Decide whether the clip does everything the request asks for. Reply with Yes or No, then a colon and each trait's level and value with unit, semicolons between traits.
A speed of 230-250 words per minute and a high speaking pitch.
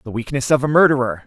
No: fast, 235 wpm; low, 135 Hz